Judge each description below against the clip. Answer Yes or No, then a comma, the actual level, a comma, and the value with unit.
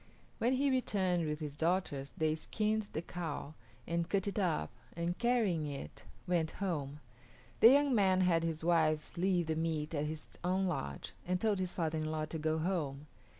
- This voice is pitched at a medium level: Yes, medium, 170 Hz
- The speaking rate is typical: Yes, average, 185 wpm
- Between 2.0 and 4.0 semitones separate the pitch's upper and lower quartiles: Yes, average, 3.4 semitones